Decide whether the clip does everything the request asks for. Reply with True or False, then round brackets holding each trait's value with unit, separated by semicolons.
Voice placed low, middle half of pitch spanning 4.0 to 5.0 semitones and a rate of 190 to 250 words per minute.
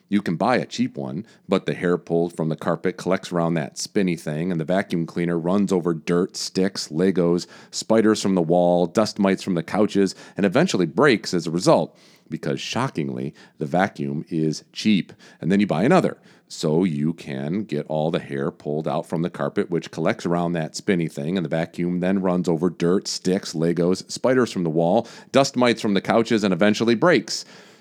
False (90 Hz; 3.5 semitones; 200 wpm)